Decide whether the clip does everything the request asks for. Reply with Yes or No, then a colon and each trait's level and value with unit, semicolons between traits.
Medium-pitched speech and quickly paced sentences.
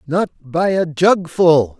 No: medium, 165 Hz; slow, 135 wpm